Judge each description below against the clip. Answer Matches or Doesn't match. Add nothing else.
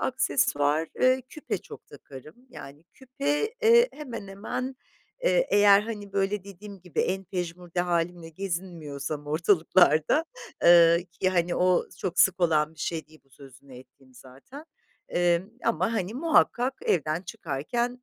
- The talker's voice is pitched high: Doesn't match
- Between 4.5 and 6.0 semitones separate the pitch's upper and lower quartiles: Matches